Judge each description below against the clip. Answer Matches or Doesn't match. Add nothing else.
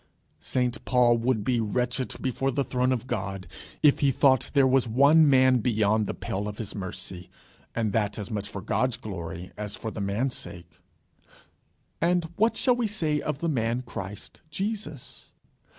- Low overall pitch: Matches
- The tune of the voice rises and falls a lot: Doesn't match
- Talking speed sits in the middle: Matches